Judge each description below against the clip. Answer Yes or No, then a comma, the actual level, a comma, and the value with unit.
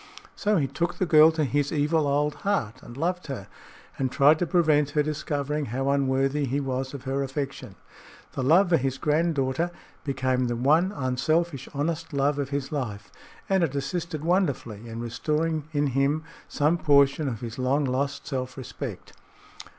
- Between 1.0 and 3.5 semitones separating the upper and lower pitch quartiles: Yes, average, 2.9 semitones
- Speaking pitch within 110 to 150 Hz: Yes, medium, 140 Hz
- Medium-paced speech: Yes, average, 170 wpm